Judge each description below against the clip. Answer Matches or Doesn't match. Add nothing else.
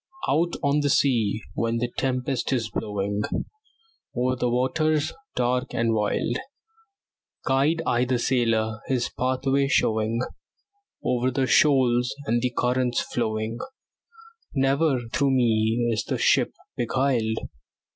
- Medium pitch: Doesn't match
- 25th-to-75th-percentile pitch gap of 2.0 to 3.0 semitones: Matches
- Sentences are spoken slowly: Matches